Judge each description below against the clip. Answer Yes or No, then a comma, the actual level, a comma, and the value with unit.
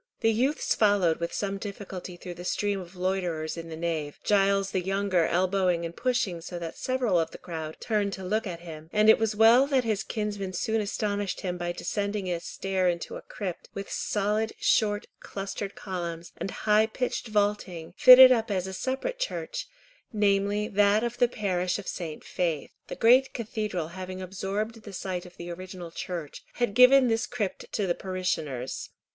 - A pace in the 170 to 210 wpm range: Yes, average, 185 wpm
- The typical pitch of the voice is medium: No, high, 195 Hz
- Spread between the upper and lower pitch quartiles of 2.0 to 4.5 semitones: Yes, average, 3.4 semitones